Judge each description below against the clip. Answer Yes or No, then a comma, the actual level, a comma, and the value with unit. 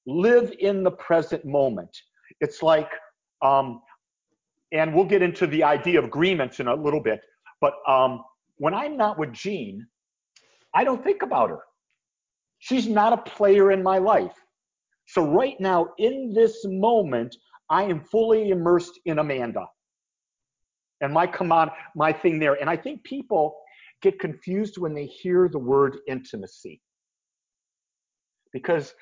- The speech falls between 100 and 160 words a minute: Yes, average, 145 wpm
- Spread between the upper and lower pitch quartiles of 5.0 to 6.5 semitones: Yes, wide, 5.6 semitones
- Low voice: No, medium, 175 Hz